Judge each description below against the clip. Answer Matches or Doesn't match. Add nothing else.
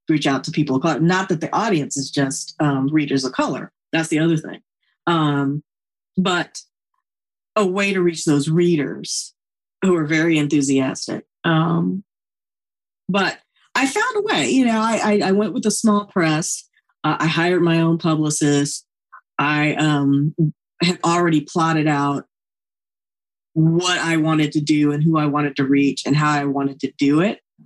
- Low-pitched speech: Doesn't match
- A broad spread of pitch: Doesn't match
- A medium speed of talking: Matches